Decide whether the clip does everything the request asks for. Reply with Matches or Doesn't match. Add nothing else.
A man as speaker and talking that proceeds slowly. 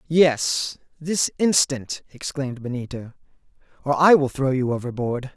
Matches